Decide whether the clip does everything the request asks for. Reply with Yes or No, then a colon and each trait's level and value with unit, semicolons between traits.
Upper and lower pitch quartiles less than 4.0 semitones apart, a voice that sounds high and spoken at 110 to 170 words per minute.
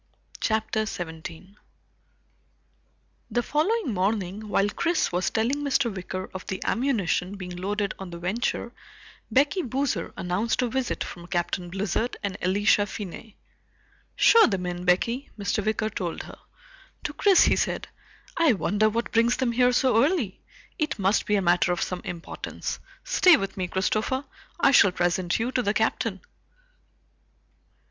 No: average, 4.9 semitones; high, 210 Hz; average, 150 wpm